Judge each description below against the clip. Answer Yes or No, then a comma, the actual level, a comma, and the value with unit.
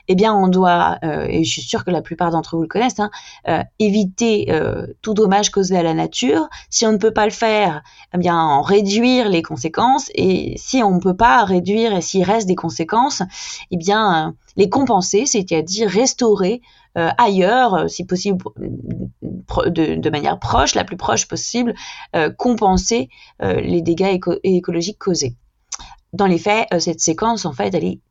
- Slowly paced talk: No, average, 190 wpm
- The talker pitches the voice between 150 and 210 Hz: Yes, high, 190 Hz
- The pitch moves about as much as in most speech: Yes, average, 4.1 semitones